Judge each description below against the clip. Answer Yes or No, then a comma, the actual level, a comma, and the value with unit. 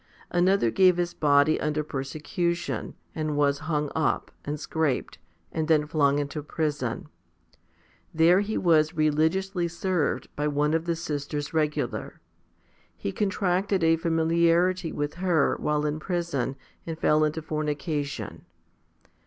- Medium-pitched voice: Yes, medium, 155 Hz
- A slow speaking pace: Yes, slow, 130 wpm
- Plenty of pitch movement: No, narrow, 2.6 semitones